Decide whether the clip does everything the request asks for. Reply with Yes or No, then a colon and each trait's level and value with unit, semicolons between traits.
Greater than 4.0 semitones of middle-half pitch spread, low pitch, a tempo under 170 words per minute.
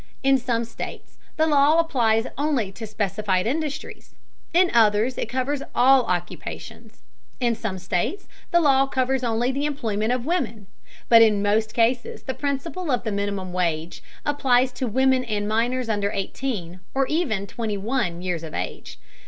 No: average, 4.5 semitones; high, 235 Hz; average, 160 wpm